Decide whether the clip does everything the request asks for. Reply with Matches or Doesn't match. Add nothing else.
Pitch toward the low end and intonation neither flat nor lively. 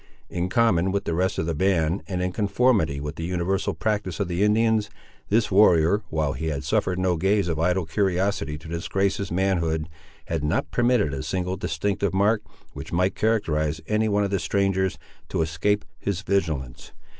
Matches